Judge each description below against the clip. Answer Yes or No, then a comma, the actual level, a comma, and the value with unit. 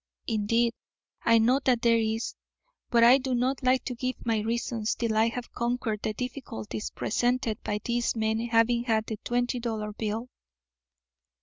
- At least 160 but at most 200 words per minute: Yes, average, 165 wpm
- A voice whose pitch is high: Yes, high, 230 Hz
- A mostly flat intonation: Yes, narrow, 1.8 semitones